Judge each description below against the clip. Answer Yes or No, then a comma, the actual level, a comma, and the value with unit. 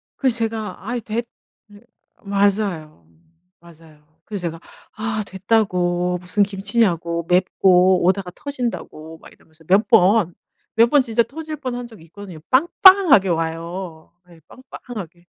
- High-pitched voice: Yes, high, 195 Hz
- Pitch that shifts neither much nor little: Yes, average, 4.9 semitones